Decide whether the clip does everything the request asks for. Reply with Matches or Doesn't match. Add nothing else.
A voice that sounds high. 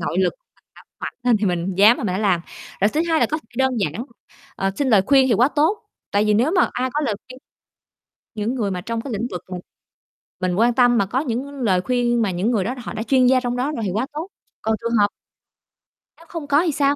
Matches